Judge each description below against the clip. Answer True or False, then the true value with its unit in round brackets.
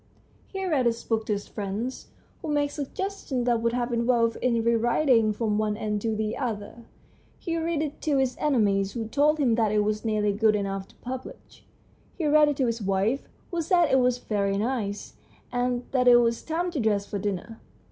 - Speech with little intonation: False (4.3 semitones)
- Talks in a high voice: True (235 Hz)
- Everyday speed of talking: False (210 wpm)